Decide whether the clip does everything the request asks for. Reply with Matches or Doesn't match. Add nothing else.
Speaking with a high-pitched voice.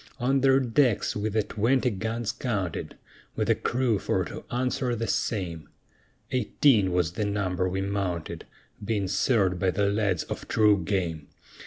Doesn't match